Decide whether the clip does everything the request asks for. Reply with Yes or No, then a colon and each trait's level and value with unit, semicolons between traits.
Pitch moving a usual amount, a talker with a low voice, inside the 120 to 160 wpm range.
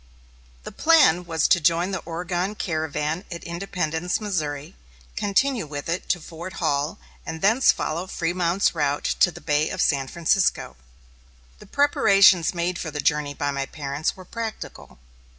No: average, 3.7 semitones; medium, 170 Hz; average, 150 wpm